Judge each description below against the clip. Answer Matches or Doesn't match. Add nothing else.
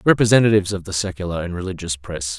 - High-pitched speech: Doesn't match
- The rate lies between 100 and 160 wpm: Doesn't match